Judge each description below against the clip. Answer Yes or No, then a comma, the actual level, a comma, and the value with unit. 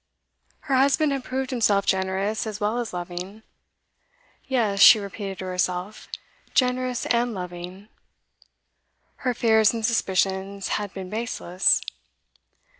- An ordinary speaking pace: No, slow, 115 wpm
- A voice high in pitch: Yes, high, 210 Hz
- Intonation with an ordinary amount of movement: Yes, average, 4.1 semitones